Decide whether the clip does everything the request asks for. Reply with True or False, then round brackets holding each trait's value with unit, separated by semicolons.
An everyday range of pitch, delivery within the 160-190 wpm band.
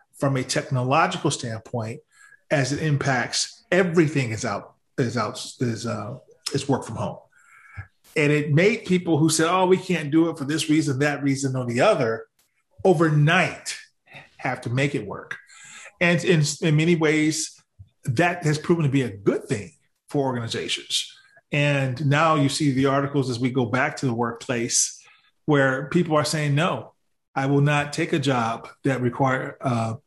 True (3.9 semitones; 170 wpm)